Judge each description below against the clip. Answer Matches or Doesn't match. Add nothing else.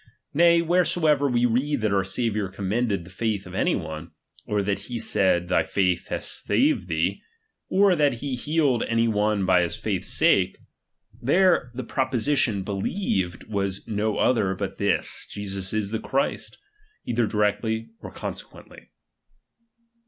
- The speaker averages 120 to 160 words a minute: Matches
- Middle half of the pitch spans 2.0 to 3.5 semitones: Doesn't match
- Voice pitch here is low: Matches